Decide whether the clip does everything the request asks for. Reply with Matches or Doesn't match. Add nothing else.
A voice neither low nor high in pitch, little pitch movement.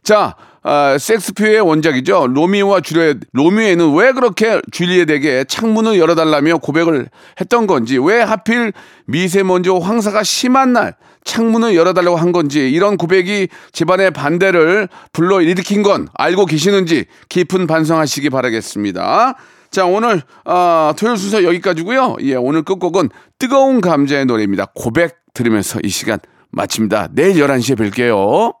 Doesn't match